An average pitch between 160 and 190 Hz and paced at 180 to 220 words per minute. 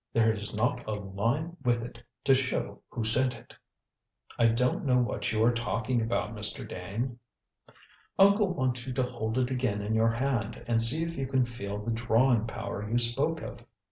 No: low, 120 Hz; average, 190 wpm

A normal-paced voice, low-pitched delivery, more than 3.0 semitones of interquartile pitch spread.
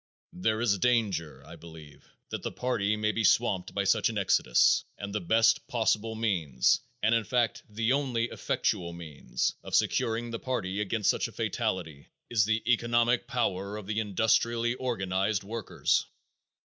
Yes: average, 160 wpm; low, 110 Hz; average, 3.6 semitones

